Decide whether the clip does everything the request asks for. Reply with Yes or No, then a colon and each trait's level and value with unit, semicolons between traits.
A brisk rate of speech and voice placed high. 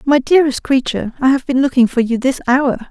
Yes: fast, 225 wpm; very high, 260 Hz